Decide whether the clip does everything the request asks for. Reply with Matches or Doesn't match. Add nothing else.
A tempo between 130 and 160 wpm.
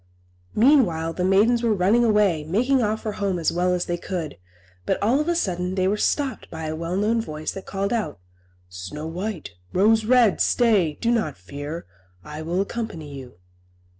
Doesn't match